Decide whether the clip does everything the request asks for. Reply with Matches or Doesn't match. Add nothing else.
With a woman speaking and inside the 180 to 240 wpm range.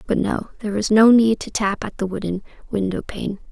Matches